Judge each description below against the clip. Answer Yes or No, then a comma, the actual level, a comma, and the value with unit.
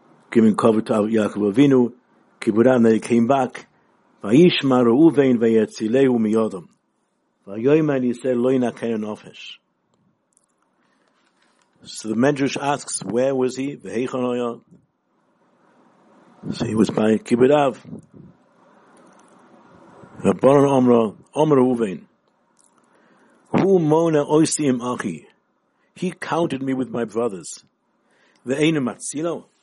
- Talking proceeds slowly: Yes, slow, 105 wpm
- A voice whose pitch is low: Yes, low, 125 Hz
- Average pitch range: Yes, average, 3.4 semitones